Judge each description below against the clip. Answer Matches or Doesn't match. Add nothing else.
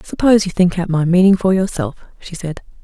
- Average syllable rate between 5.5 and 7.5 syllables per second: Matches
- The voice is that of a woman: Matches